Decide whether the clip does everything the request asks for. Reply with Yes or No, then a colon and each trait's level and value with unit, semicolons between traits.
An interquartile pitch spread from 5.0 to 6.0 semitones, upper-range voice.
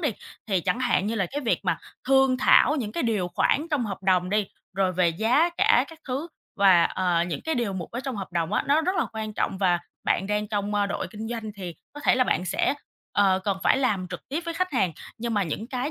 Yes: wide, 5.5 semitones; high, 215 Hz